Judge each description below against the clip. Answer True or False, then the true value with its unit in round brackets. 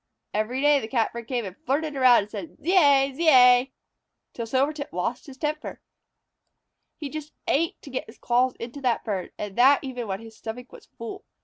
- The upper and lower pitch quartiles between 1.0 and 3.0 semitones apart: False (3.7 semitones)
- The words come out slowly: False (185 wpm)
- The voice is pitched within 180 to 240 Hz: False (255 Hz)